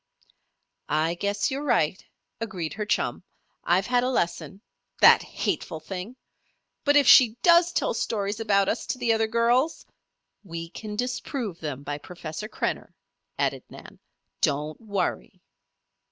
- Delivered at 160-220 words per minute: No, average, 140 wpm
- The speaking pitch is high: Yes, high, 210 Hz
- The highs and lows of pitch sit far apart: Yes, wide, 5.9 semitones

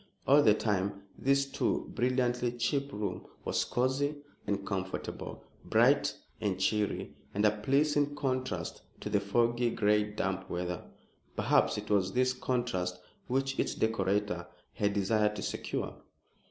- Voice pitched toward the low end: Yes, low, 110 Hz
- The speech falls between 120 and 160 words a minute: Yes, slow, 135 wpm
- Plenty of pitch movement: No, average, 4.4 semitones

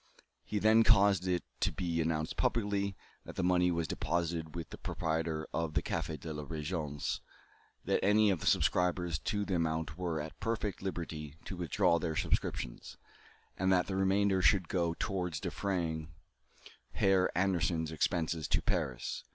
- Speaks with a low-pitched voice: Yes, very low, 85 Hz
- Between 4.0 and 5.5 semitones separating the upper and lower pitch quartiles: No, average, 3.1 semitones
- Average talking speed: Yes, average, 160 wpm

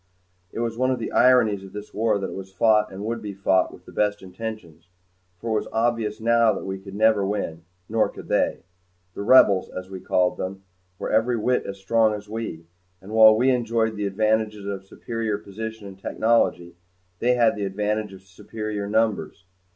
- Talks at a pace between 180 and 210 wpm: Yes, average, 200 wpm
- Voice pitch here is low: Yes, low, 105 Hz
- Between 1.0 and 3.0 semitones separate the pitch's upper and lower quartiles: Yes, narrow, 2.6 semitones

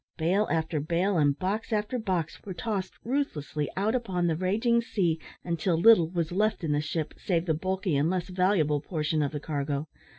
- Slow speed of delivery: No, average, 190 wpm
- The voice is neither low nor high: Yes, medium, 175 Hz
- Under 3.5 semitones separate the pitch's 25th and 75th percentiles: No, average, 4.2 semitones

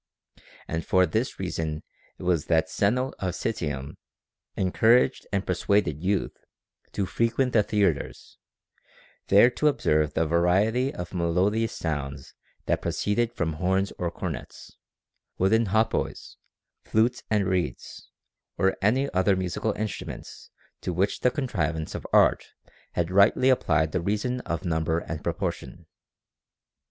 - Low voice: Yes, very low, 95 Hz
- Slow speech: Yes, slow, 125 wpm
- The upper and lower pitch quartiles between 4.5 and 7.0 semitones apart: Yes, average, 5.0 semitones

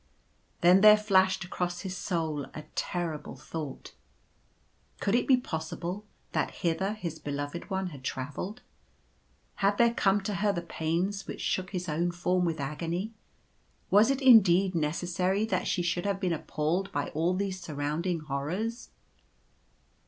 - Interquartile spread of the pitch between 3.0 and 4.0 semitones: Yes, average, 3.6 semitones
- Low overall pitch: No, medium, 180 Hz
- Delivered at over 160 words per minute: No, average, 150 wpm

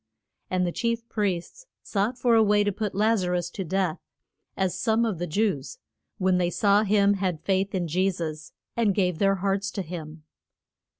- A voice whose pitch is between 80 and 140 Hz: No, high, 195 Hz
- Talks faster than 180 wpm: Yes, average, 190 wpm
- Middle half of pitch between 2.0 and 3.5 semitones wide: Yes, average, 2.7 semitones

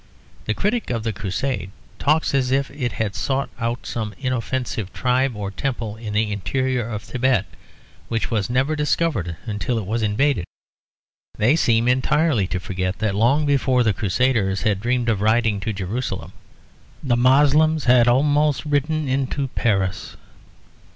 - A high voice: No, low, 120 Hz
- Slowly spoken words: No, average, 150 wpm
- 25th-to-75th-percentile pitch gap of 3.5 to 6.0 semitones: Yes, average, 4.3 semitones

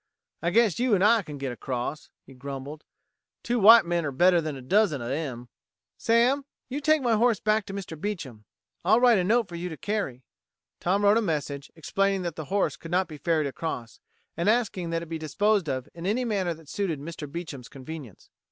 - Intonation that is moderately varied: No, wide, 6.2 semitones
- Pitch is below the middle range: No, medium, 170 Hz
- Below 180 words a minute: No, fast, 205 wpm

